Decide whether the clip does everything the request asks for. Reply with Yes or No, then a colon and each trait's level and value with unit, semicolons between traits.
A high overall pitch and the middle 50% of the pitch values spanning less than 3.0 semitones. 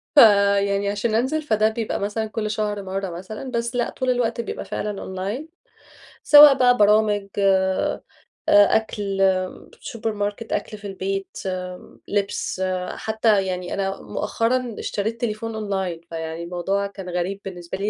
Yes: high, 205 Hz; narrow, 2.6 semitones